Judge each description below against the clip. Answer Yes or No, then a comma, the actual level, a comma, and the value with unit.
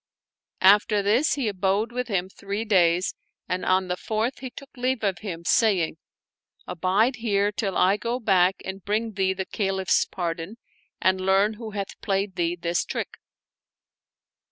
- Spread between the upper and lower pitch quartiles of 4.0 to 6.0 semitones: No, average, 2.8 semitones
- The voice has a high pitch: Yes, high, 195 Hz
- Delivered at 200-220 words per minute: No, average, 160 wpm